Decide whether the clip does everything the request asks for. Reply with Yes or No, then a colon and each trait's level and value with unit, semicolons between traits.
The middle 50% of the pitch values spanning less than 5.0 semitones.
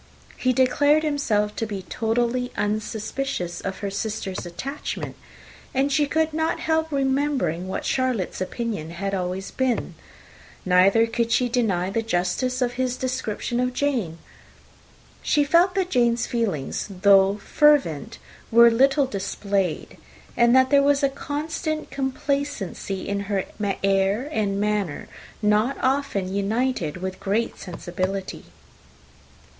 No: wide, 5.6 semitones